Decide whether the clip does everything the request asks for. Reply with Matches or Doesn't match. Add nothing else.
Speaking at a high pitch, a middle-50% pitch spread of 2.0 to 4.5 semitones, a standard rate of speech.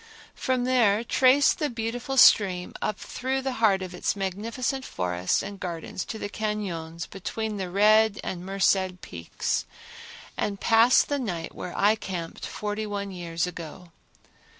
Matches